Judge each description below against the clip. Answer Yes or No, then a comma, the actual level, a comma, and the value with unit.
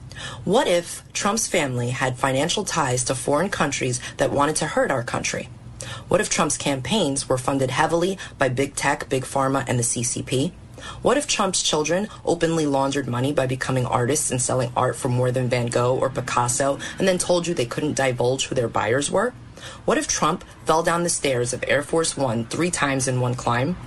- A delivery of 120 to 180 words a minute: No, average, 195 wpm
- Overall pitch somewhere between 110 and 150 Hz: Yes, low, 135 Hz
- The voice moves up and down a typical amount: Yes, average, 4.1 semitones